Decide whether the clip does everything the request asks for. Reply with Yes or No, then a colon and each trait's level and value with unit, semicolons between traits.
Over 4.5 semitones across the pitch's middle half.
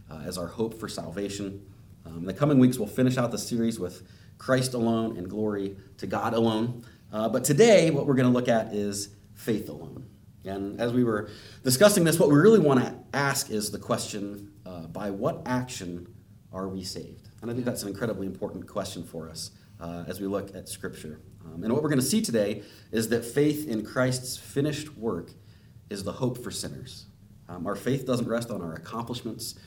No: average, 3.9 semitones